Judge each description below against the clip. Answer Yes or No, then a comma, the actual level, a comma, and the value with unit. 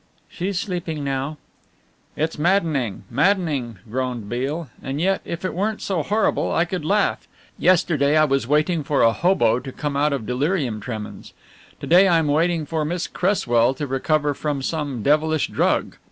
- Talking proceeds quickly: No, average, 170 wpm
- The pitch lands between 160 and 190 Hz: No, medium, 150 Hz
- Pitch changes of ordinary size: Yes, average, 4.5 semitones